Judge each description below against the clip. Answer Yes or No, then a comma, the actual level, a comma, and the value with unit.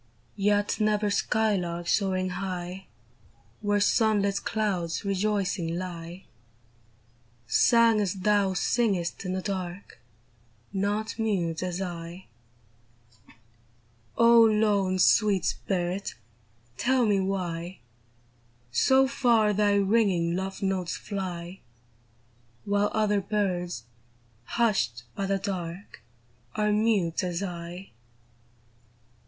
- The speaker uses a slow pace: Yes, slow, 95 wpm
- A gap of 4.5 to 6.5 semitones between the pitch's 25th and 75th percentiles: No, average, 2.9 semitones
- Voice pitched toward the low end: No, high, 195 Hz